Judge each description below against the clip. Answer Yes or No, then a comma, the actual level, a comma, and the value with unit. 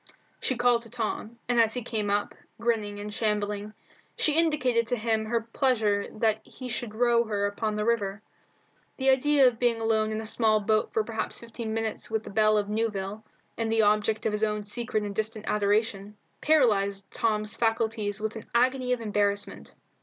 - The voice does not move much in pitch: Yes, narrow, 1.9 semitones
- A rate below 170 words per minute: No, average, 185 wpm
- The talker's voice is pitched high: Yes, high, 220 Hz